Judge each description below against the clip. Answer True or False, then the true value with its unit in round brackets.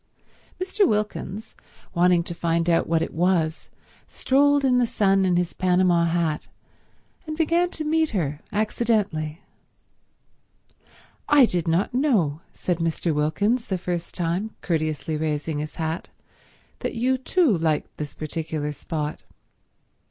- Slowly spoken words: True (130 wpm)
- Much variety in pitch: True (5.9 semitones)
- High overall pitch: False (175 Hz)